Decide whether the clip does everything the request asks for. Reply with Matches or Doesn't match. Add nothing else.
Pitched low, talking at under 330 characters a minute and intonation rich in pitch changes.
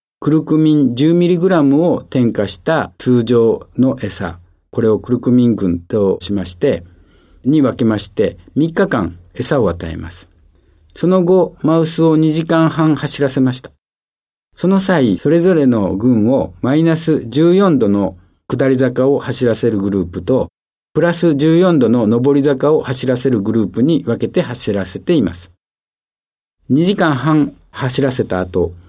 Matches